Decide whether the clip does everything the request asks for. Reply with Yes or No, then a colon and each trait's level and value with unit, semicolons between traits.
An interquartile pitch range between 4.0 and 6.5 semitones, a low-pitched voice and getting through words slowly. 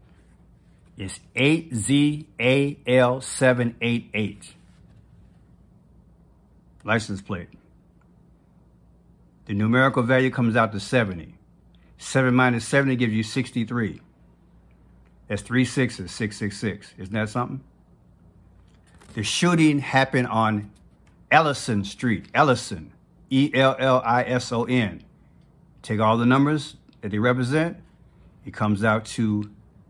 Yes: average, 4.4 semitones; low, 115 Hz; slow, 100 wpm